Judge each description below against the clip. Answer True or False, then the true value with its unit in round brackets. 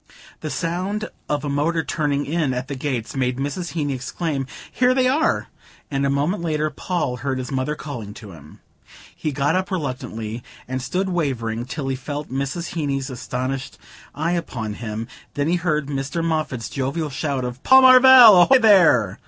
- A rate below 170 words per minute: False (175 wpm)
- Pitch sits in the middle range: True (145 Hz)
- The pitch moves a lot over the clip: False (4.7 semitones)